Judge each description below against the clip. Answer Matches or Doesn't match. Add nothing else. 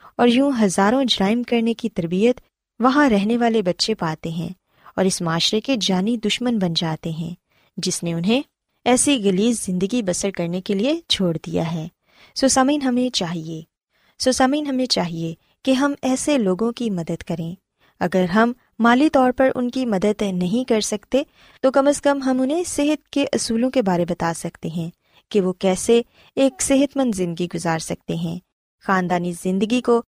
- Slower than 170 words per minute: Doesn't match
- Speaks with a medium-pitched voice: Doesn't match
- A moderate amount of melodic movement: Doesn't match